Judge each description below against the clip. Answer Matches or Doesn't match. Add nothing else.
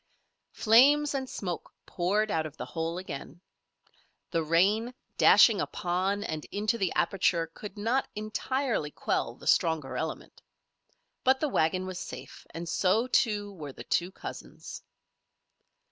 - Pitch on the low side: Doesn't match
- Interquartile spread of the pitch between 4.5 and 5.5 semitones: Matches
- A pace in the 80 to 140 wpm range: Matches